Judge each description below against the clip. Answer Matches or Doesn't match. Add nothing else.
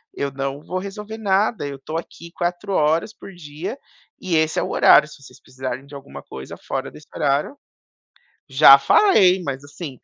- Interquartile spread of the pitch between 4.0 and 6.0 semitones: Matches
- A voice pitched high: Doesn't match